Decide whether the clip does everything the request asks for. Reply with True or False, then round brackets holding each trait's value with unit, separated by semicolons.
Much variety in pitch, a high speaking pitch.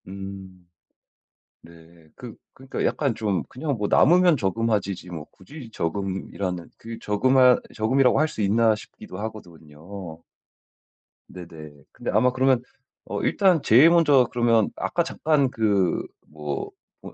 False (6.0 semitones; 110 Hz)